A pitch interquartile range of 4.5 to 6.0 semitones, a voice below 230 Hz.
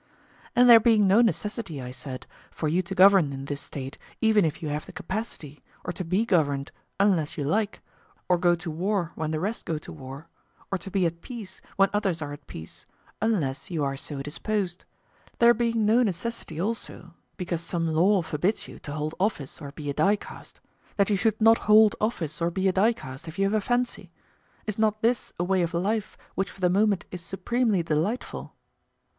Yes: average, 5.2 semitones; medium, 185 Hz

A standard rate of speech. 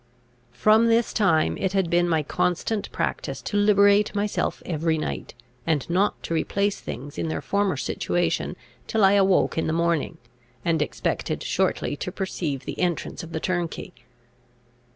Yes: average, 155 wpm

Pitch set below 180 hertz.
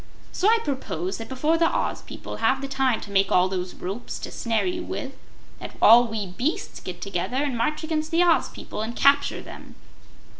No: very high, 255 Hz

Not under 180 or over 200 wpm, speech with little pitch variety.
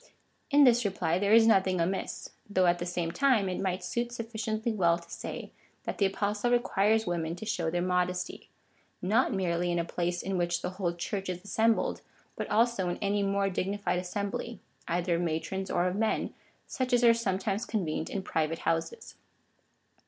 No: average, 185 wpm; average, 3.8 semitones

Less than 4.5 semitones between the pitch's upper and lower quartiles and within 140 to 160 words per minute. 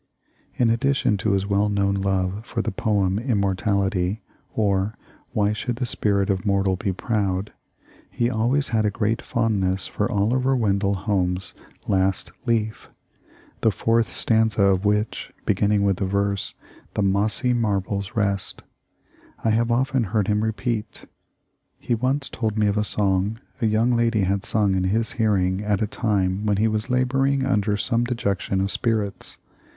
Yes: narrow, 2.6 semitones; average, 155 wpm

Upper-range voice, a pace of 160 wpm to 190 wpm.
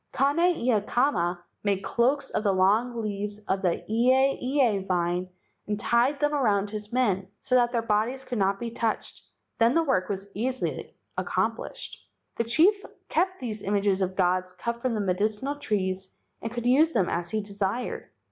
Yes: high, 220 Hz; average, 170 wpm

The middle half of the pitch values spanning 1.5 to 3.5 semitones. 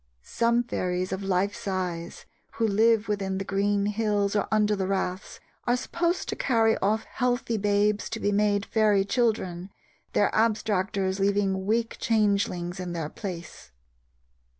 Yes: narrow, 2.6 semitones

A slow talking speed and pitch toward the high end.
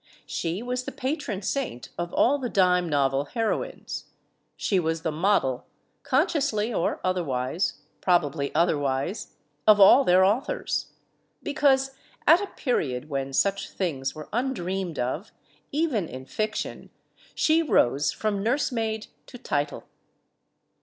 Yes: slow, 125 wpm; high, 195 Hz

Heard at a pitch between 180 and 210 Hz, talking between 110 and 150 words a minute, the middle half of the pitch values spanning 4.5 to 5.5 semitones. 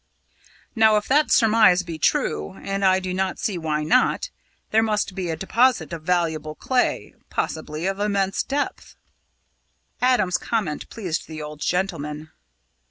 Yes: medium, 185 Hz; average, 145 wpm; average, 5.2 semitones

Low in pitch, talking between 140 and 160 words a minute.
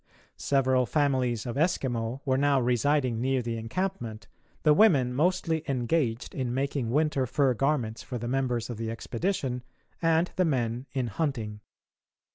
Yes: low, 130 Hz; average, 145 wpm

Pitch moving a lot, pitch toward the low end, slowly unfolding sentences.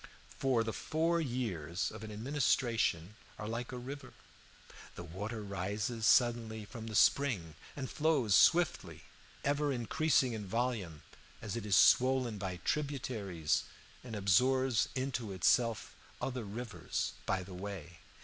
No: average, 4.5 semitones; low, 115 Hz; slow, 130 wpm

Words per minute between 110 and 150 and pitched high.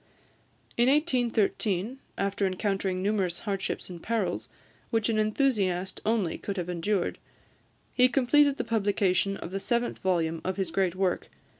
Yes: average, 140 wpm; high, 200 Hz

